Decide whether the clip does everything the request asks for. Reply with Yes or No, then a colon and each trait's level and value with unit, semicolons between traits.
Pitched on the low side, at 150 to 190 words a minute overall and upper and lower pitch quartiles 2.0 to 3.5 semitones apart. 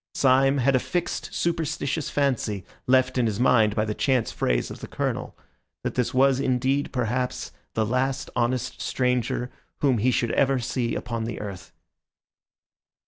Yes: low, 125 Hz; average, 155 wpm; narrow, 2.5 semitones